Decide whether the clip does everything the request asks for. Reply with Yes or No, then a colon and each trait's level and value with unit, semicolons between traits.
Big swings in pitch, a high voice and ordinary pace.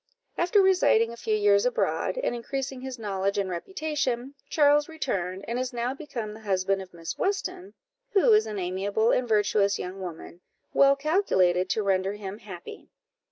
Yes: wide, 6.4 semitones; high, 220 Hz; average, 165 wpm